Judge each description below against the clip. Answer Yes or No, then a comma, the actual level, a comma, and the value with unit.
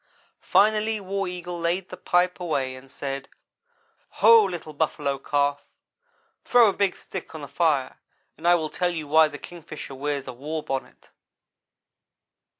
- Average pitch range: Yes, average, 4.1 semitones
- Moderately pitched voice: Yes, medium, 160 Hz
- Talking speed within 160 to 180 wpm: No, average, 150 wpm